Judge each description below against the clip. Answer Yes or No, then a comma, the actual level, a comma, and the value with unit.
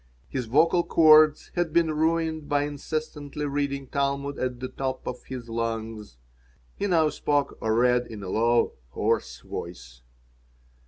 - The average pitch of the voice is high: No, medium, 140 Hz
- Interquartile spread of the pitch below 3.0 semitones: No, average, 4.9 semitones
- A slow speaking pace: No, average, 145 wpm